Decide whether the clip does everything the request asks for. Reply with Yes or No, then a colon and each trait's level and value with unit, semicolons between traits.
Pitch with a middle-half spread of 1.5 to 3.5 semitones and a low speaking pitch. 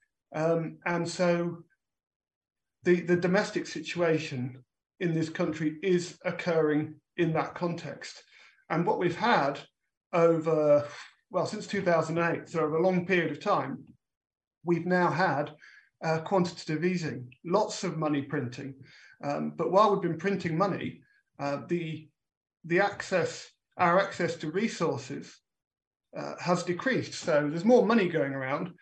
No: average, 2.8 semitones; medium, 170 Hz